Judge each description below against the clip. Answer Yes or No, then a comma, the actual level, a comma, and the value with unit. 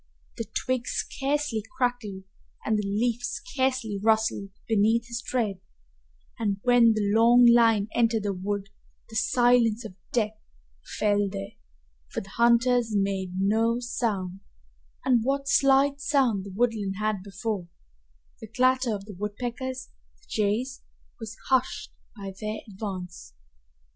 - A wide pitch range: No, average, 3.3 semitones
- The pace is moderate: No, slow, 130 wpm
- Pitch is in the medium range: No, high, 225 Hz